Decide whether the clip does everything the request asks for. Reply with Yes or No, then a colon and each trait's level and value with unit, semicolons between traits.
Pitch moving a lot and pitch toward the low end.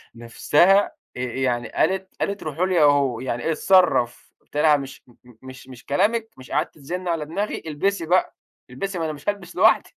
No: wide, 5.9 semitones; medium, 150 Hz